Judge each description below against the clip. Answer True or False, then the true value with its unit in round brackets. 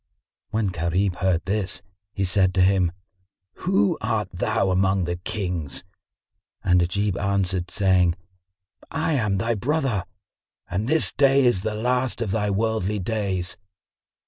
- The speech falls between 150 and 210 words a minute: False (135 wpm)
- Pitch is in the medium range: False (100 Hz)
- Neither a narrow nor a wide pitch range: True (3.3 semitones)